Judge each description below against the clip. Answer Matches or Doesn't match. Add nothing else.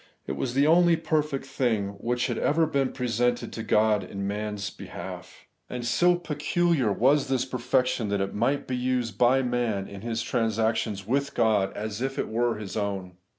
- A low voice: Matches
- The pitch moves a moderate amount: Matches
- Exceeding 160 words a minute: Matches